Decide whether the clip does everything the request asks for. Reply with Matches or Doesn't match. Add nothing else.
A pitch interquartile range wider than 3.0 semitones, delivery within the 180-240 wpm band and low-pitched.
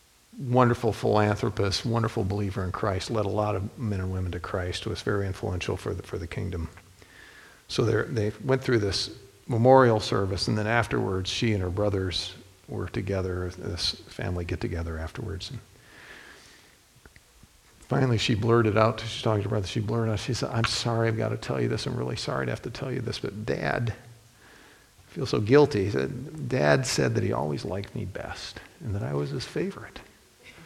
Matches